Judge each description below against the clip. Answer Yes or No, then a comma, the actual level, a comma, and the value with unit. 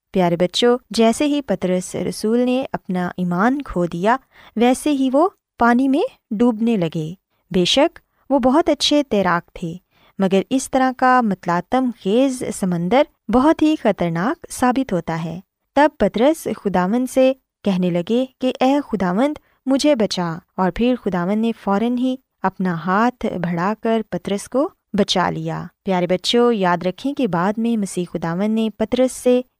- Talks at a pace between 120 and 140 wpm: No, average, 150 wpm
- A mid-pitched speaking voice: No, high, 225 Hz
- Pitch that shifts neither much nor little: No, wide, 6.0 semitones